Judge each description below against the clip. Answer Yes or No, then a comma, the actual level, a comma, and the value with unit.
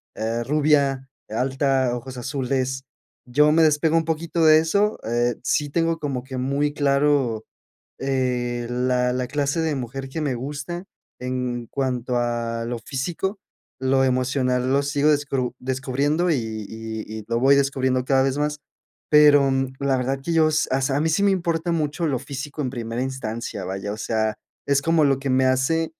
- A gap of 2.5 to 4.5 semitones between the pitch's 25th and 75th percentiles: Yes, average, 2.9 semitones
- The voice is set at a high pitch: No, low, 135 Hz